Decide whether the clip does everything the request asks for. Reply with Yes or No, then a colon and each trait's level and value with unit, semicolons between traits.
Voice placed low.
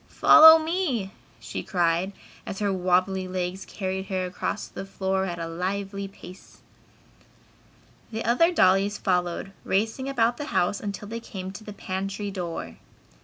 No: high, 195 Hz